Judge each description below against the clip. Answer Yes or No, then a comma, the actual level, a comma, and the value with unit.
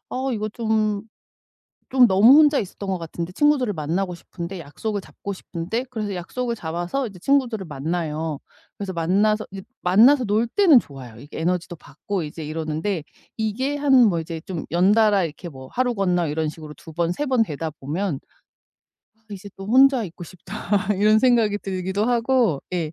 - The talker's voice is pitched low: No, high, 195 Hz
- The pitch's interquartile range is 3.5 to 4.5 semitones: No, average, 5.2 semitones